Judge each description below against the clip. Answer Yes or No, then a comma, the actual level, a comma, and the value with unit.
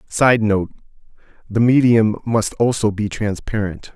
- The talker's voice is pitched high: No, low, 110 Hz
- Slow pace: Yes, slow, 105 wpm